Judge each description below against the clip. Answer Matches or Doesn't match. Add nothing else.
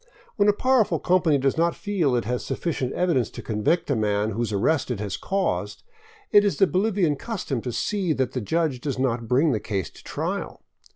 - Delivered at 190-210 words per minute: Matches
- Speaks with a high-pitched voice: Doesn't match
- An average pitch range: Doesn't match